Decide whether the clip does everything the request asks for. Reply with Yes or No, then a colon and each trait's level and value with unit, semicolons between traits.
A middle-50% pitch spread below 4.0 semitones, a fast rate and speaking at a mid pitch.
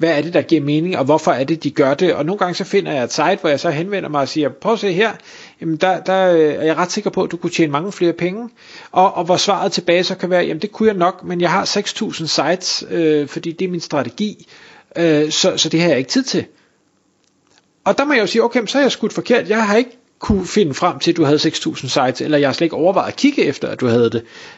No: average, 4.3 semitones; fast, 285 wpm; medium, 175 Hz